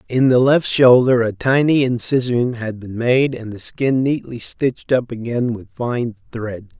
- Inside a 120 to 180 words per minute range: Yes, average, 175 wpm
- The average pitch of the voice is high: No, low, 120 Hz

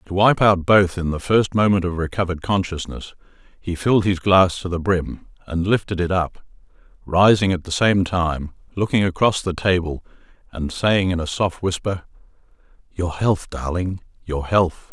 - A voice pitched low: Yes, very low, 90 Hz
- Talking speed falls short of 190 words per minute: Yes, average, 170 wpm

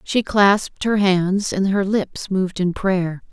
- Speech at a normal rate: Yes, average, 180 wpm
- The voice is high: Yes, high, 195 Hz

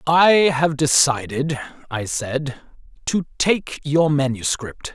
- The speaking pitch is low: No, medium, 145 Hz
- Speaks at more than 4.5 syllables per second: No, 3.3 syllables/s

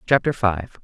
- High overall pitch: No, low, 105 Hz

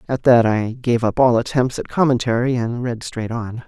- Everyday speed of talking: No, fast, 210 wpm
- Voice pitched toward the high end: No, low, 120 Hz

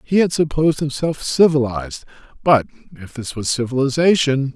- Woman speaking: No, male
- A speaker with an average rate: No, slow, 130 wpm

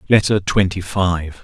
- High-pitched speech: No, very low, 95 Hz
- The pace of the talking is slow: Yes, slow, 125 wpm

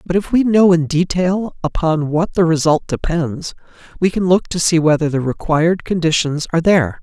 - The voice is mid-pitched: Yes, medium, 165 Hz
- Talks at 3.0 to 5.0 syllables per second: No, 5.2 syllables/s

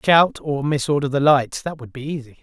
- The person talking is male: Yes, male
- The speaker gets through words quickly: Yes, fast, 245 wpm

